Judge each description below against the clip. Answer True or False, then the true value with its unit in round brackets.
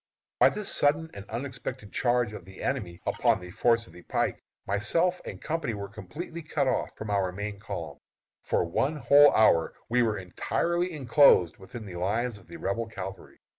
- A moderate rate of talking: True (180 wpm)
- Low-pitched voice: True (115 Hz)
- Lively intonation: True (6.4 semitones)